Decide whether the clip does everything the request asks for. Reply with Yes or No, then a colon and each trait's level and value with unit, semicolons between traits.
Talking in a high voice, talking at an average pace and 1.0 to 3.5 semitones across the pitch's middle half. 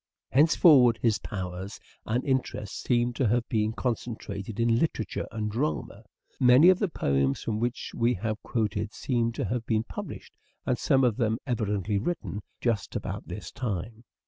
No: low, 115 Hz; average, 165 wpm; average, 2.8 semitones